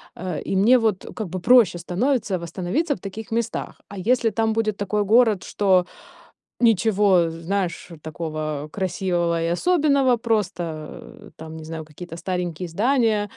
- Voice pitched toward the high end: Yes, high, 195 Hz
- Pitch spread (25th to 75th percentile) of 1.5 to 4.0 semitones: No, average, 4.7 semitones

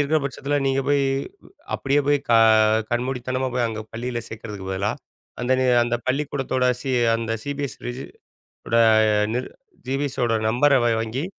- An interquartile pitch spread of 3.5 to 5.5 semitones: No, average, 2.9 semitones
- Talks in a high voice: No, low, 130 Hz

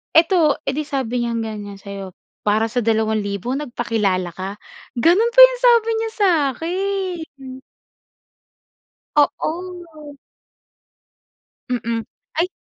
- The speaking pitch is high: Yes, very high, 250 Hz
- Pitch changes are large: Yes, wide, 8.5 semitones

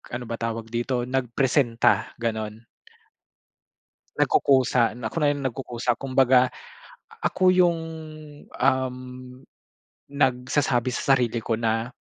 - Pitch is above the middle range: No, low, 125 Hz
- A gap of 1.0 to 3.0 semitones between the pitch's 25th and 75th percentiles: Yes, narrow, 2.4 semitones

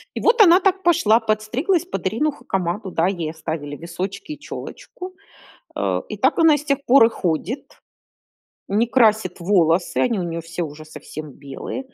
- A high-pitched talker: Yes, high, 210 Hz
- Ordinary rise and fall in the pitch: No, wide, 8.8 semitones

